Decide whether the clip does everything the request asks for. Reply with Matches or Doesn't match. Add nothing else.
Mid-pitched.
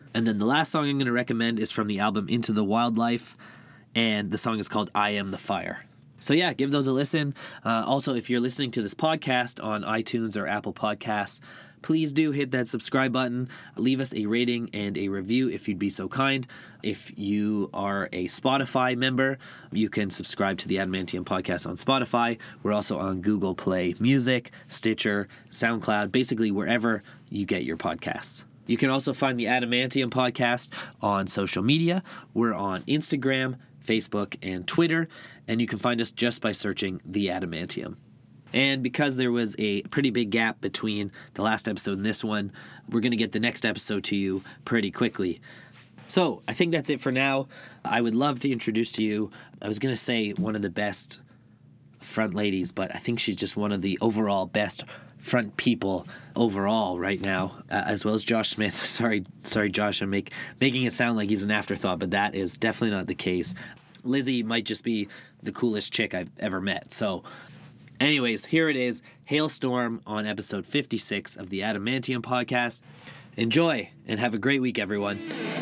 Doesn't match